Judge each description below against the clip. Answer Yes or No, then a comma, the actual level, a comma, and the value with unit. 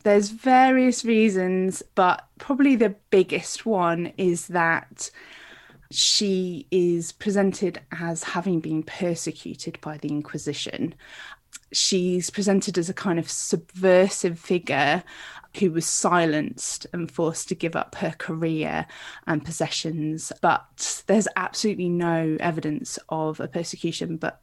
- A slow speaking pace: Yes, slow, 120 wpm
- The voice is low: No, medium, 175 Hz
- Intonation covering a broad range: No, average, 3.2 semitones